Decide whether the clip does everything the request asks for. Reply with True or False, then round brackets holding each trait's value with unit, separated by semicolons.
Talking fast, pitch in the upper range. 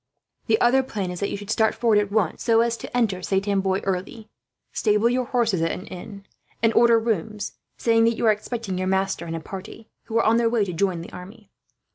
True (230 wpm; 210 Hz)